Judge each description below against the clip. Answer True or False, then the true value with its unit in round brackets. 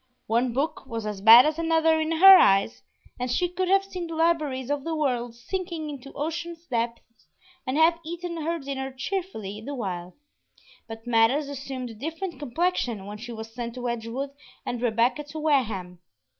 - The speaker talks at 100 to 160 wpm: False (175 wpm)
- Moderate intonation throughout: False (5.9 semitones)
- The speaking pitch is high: True (270 Hz)